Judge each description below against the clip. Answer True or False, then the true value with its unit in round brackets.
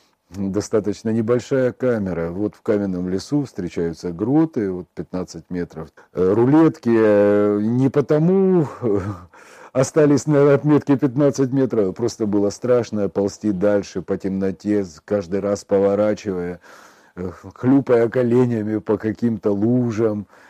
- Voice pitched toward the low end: True (105 Hz)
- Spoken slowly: True (100 wpm)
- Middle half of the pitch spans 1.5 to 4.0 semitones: False (4.4 semitones)